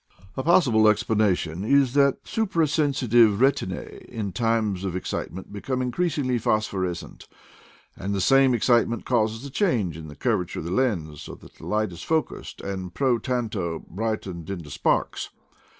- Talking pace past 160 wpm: No, average, 150 wpm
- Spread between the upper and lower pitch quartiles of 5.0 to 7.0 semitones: Yes, wide, 5.6 semitones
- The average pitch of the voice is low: Yes, low, 110 Hz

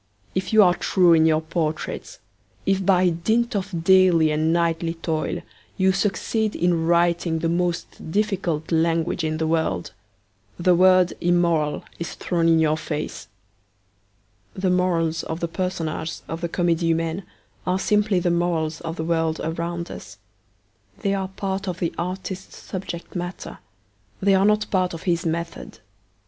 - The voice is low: No, medium, 170 Hz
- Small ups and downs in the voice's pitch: Yes, narrow, 2.3 semitones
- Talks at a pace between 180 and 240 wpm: No, average, 155 wpm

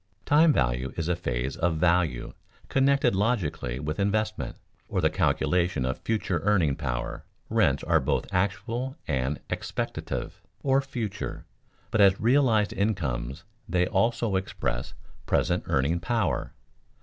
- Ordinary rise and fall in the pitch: No, wide, 7.8 semitones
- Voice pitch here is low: Yes, very low, 90 Hz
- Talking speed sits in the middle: No, slow, 125 wpm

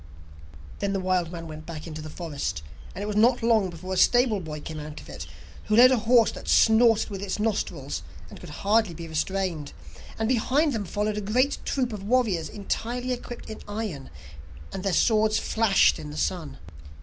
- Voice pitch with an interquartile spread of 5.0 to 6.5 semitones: Yes, average, 5.3 semitones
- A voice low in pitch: No, high, 205 Hz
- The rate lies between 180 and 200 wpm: Yes, average, 195 wpm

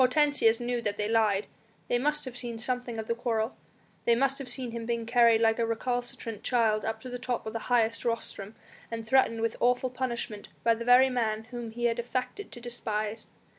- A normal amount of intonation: No, narrow, 1.7 semitones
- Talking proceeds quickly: Yes, fast, 210 wpm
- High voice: Yes, high, 235 Hz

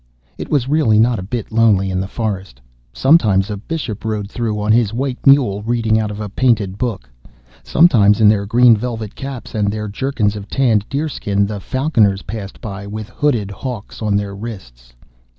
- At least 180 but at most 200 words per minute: Yes, average, 185 wpm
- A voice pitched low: Yes, low, 110 Hz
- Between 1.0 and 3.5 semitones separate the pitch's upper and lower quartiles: Yes, average, 3.1 semitones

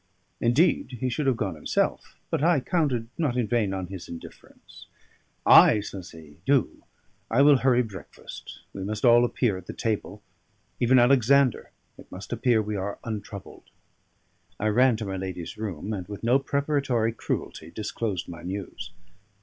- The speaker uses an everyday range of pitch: Yes, average, 4.8 semitones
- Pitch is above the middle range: No, low, 110 Hz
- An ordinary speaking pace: Yes, average, 160 wpm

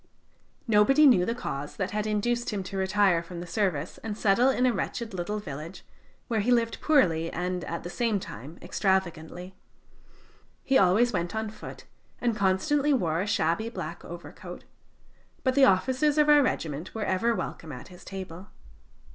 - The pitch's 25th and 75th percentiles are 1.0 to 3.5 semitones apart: No, average, 5.1 semitones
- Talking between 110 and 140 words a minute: No, average, 170 wpm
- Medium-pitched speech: No, high, 200 Hz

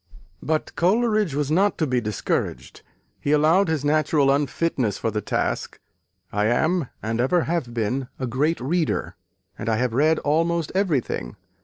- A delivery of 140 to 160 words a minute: Yes, average, 150 wpm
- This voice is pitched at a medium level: Yes, medium, 150 Hz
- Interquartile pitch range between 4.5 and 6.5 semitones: Yes, average, 5.2 semitones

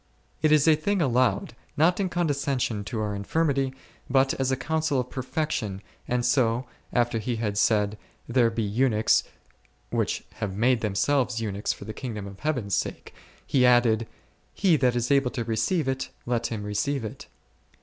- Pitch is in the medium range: No, low, 125 Hz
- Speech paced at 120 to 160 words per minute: No, average, 170 wpm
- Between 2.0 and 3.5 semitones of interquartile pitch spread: No, average, 4.1 semitones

